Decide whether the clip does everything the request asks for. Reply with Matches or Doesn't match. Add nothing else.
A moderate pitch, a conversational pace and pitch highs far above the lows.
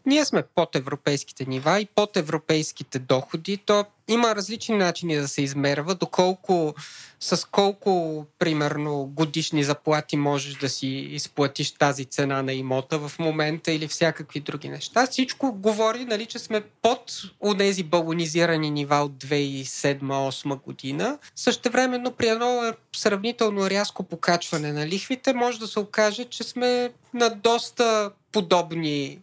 Matches